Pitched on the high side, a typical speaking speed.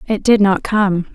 No: high, 200 Hz; fast, 210 wpm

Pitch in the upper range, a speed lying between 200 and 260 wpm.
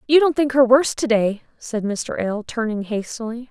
Yes: high, 235 Hz; fast, 205 wpm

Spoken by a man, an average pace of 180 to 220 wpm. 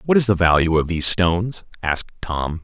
Yes: male; fast, 205 wpm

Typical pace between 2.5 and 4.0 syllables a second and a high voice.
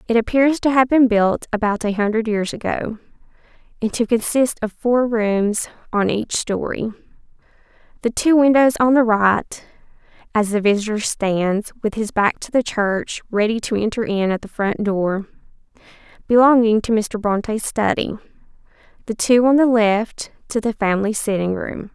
Yes: 3.5 syllables/s; high, 220 Hz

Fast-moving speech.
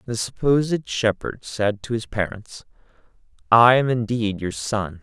No: average, 145 wpm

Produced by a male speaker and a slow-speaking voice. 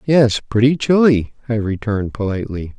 Yes: male; slow, 130 wpm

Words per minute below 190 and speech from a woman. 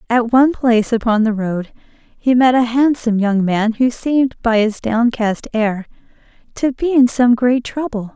Yes: average, 175 wpm; female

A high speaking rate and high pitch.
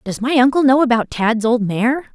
Yes: fast, 225 wpm; high, 245 Hz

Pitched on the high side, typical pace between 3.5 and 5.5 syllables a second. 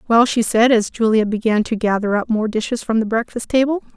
No: high, 225 Hz; 5.7 syllables/s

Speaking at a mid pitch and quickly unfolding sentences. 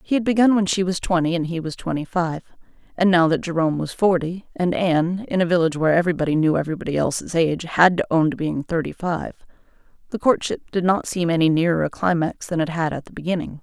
Yes: medium, 170 Hz; fast, 225 wpm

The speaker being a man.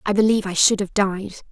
No: female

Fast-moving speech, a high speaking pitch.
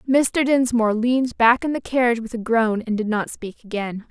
Yes: fast, 220 wpm; high, 235 Hz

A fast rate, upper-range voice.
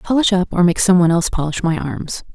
No: fast, 255 wpm; medium, 175 Hz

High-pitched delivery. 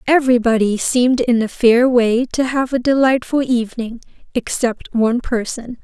Yes: high, 245 Hz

